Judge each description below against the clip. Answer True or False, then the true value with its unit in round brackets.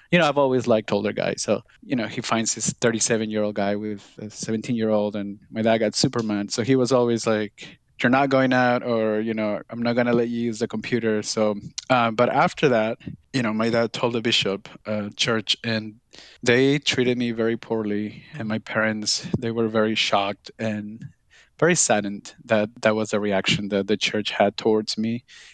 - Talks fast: True (210 wpm)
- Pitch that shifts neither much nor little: False (2.3 semitones)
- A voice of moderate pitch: False (115 Hz)